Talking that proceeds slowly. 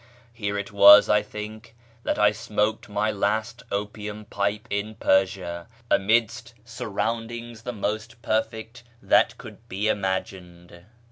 Yes: slow, 125 wpm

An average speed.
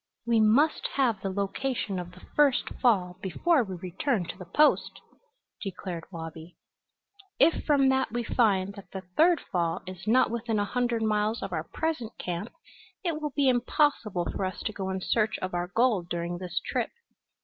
Yes: average, 180 wpm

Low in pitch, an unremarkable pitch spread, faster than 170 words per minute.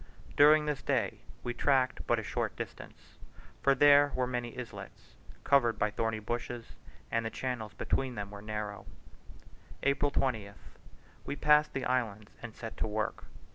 No: low, 120 Hz; average, 4.1 semitones; average, 155 wpm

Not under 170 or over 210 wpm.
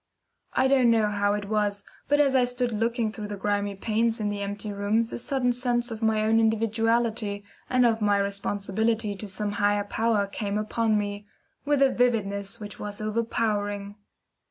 Yes: average, 180 wpm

